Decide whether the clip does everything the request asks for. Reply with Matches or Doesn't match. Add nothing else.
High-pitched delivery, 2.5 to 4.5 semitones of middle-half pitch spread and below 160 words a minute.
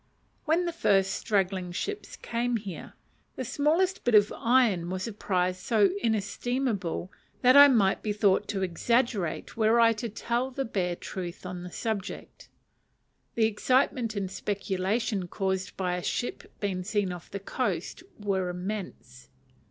Matches